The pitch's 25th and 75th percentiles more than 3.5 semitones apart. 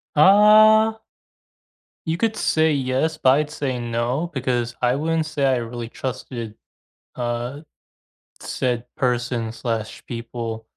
Yes: average, 4.7 semitones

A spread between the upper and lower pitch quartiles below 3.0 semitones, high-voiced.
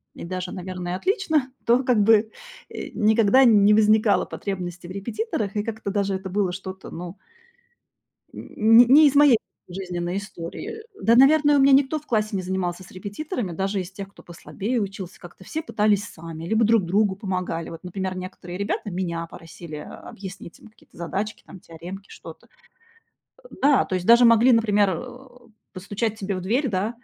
No: average, 3.8 semitones; high, 200 Hz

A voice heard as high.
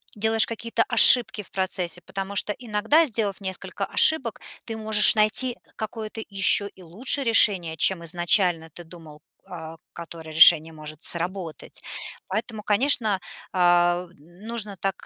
Yes: high, 195 Hz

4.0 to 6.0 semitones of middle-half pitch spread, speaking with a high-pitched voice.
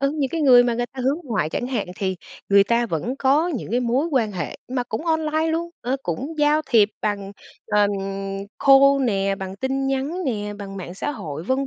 Yes: average, 5.2 semitones; high, 245 Hz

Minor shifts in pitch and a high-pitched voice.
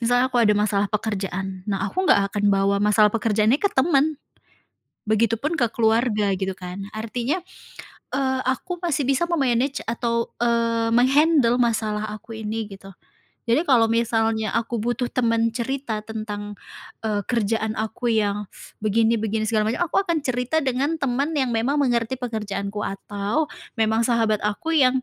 No: average, 3.2 semitones; high, 230 Hz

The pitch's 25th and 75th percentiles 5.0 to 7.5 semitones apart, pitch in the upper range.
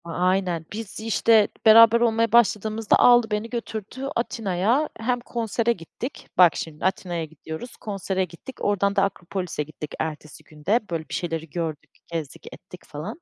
Yes: average, 5.3 semitones; high, 195 Hz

